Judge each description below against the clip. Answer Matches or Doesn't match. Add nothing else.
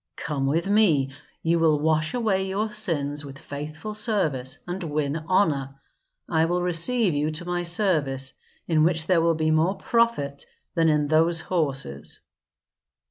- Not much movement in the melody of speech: Doesn't match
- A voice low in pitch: Doesn't match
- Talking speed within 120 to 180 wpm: Matches